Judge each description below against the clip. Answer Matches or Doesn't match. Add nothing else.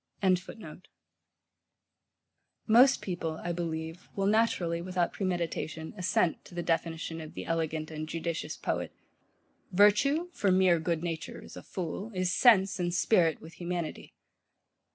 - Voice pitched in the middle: Matches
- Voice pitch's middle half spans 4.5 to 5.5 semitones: Doesn't match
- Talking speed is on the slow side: Matches